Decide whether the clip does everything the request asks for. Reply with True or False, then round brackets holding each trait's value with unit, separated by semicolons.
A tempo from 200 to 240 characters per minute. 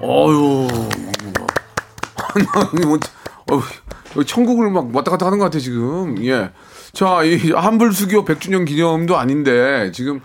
True (225 characters per minute)